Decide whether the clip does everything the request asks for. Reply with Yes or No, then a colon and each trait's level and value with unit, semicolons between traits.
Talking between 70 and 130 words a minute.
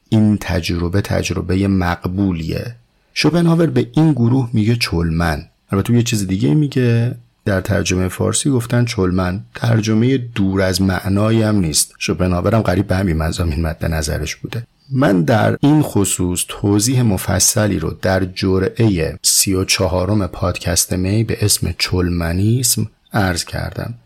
Yes: average, 125 wpm